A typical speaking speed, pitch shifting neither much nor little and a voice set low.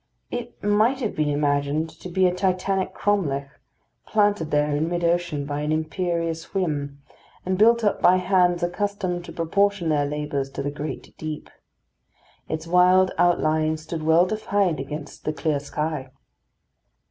No: average, 150 wpm; average, 3.8 semitones; medium, 165 Hz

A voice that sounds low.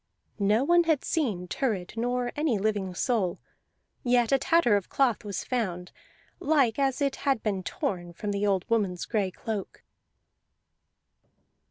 No: high, 225 Hz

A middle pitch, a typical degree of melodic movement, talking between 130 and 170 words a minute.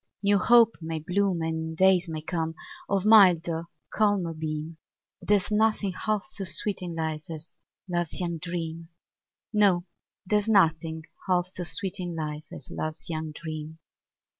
Yes: medium, 175 Hz; average, 3.5 semitones; average, 150 wpm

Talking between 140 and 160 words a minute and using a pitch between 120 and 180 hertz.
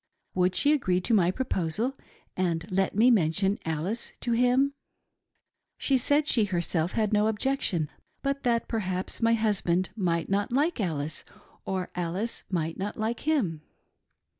No: average, 150 wpm; high, 200 Hz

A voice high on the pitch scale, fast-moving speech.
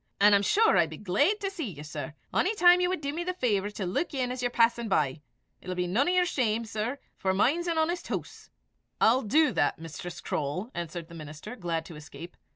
Yes: high, 220 Hz; fast, 230 wpm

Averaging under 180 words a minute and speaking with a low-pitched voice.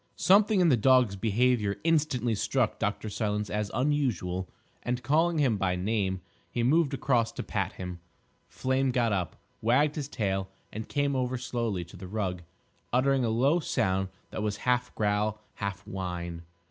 Yes: average, 160 wpm; low, 115 Hz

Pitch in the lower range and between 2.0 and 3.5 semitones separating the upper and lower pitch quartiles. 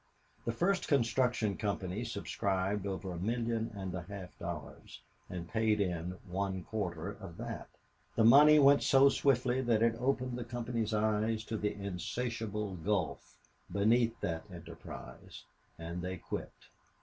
No: low, 105 Hz; average, 4.2 semitones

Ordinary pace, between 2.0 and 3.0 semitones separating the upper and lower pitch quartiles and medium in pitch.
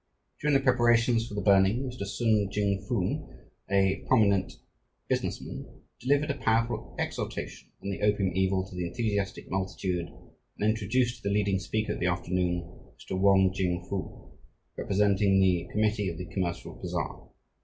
No: average, 155 wpm; average, 2.7 semitones; low, 100 Hz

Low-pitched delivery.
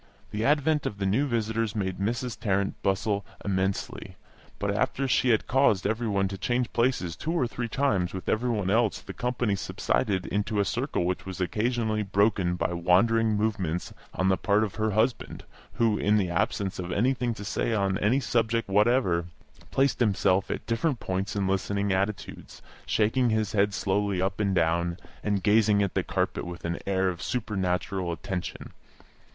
Yes: low, 105 Hz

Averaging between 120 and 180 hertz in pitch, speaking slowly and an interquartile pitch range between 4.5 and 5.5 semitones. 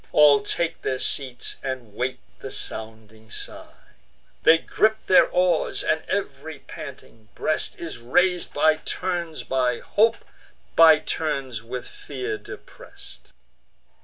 Yes: medium, 140 Hz; slow, 120 wpm; average, 4.9 semitones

